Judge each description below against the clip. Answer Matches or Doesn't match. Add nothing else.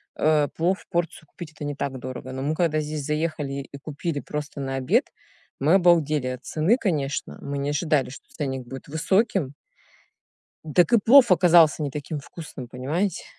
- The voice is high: Doesn't match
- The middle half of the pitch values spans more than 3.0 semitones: Matches